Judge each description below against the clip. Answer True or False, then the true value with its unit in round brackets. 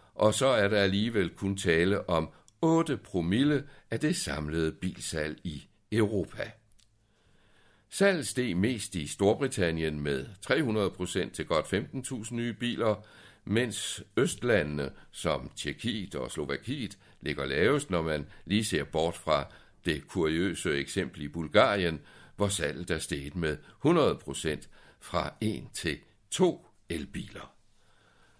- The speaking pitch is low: True (100 Hz)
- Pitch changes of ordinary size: False (5.7 semitones)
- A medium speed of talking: False (125 wpm)